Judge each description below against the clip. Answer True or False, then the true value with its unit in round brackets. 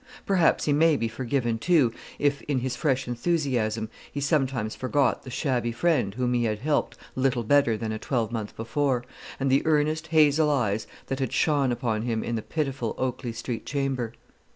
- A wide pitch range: False (3.7 semitones)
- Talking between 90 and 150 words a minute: False (175 wpm)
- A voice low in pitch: True (130 Hz)